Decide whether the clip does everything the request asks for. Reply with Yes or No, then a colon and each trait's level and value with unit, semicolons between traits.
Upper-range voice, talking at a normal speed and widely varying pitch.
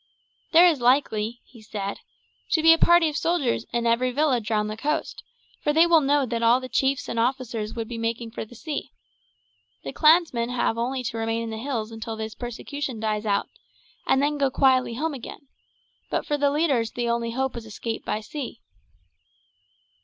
No: high, 245 Hz; average, 190 wpm; average, 4.0 semitones